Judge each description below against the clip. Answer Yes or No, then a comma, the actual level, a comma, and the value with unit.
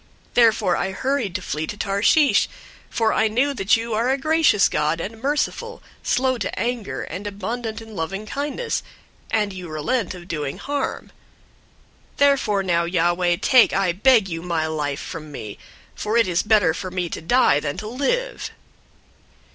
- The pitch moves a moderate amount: No, wide, 6.1 semitones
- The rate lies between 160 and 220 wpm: Yes, average, 170 wpm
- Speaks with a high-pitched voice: Yes, high, 205 Hz